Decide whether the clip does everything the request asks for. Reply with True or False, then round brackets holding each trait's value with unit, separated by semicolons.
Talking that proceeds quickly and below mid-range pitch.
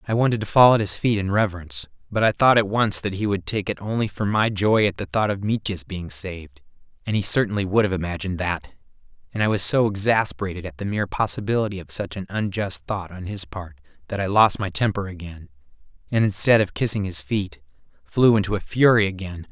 True (220 wpm; 100 Hz)